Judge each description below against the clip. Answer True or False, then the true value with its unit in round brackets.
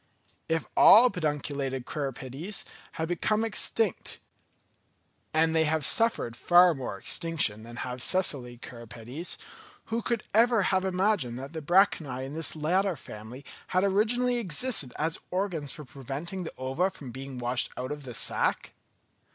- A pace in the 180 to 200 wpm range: False (145 wpm)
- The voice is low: False (160 Hz)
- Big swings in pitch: True (6.4 semitones)